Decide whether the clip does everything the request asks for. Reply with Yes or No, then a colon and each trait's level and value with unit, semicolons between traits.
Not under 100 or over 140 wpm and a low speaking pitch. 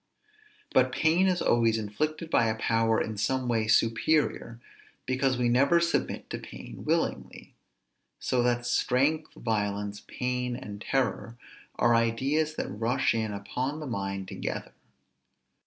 Yes: slow, 135 wpm; low, 120 Hz